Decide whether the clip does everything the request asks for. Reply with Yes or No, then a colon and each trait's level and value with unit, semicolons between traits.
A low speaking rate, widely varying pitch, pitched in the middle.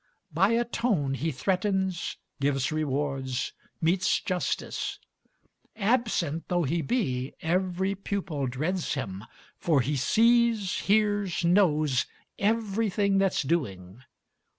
Yes: slow, 105 wpm; wide, 6.2 semitones; medium, 175 Hz